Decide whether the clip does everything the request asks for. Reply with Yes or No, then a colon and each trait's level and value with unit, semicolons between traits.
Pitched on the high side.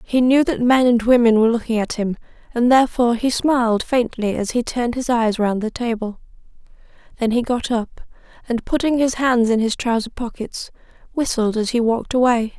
Yes: high, 235 Hz